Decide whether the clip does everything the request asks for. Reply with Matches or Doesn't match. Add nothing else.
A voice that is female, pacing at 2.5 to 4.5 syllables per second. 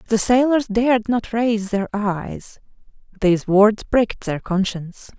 Matches